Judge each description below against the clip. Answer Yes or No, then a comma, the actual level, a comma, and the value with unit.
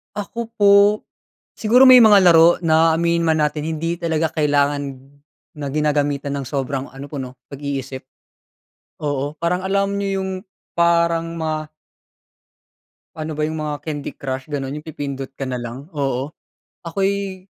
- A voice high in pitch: No, medium, 155 Hz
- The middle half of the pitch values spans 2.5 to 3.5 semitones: Yes, average, 3.2 semitones